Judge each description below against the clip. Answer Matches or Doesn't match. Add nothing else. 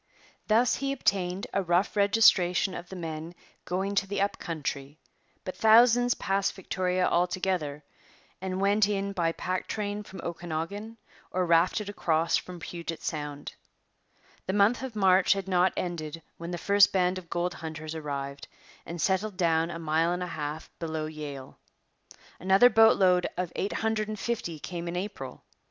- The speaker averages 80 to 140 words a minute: Doesn't match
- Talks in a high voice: Doesn't match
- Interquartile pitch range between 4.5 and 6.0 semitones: Doesn't match